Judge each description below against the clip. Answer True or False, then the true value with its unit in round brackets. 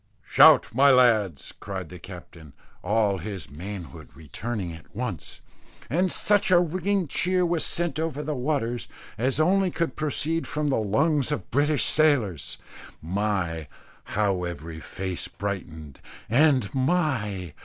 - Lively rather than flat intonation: True (8.9 semitones)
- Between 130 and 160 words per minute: True (135 wpm)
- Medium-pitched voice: False (115 Hz)